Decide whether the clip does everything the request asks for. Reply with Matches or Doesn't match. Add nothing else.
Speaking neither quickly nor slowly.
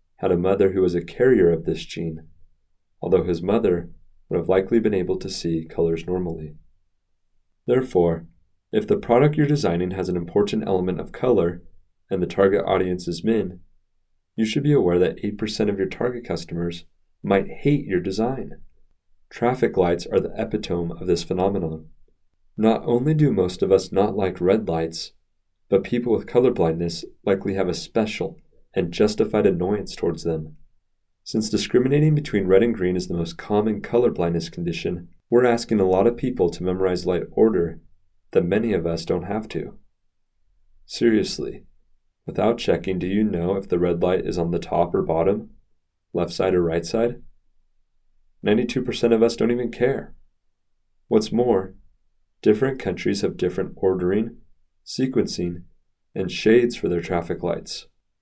Matches